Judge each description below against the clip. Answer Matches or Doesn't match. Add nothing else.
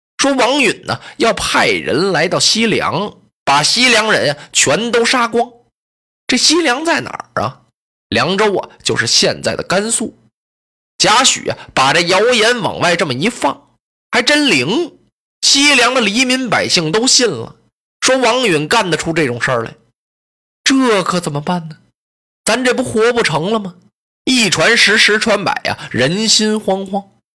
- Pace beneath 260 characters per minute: Matches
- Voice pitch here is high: Matches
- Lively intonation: Doesn't match